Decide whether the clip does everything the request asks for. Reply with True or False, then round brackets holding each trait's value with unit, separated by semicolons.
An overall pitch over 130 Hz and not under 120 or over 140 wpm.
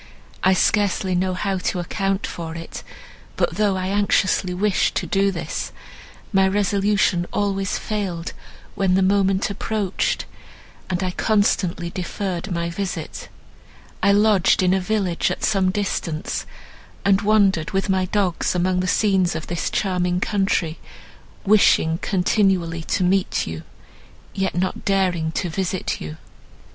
True (190 Hz; 135 wpm)